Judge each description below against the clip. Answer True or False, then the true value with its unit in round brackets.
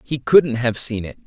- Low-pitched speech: True (120 Hz)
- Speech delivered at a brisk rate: True (235 wpm)